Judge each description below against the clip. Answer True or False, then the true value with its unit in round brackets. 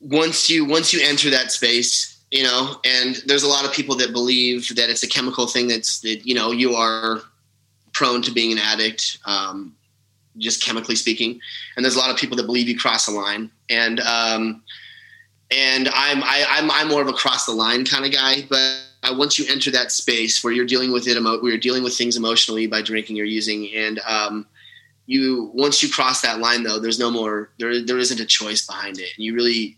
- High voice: False (120 Hz)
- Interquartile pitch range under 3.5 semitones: True (2.6 semitones)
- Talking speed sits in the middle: False (220 wpm)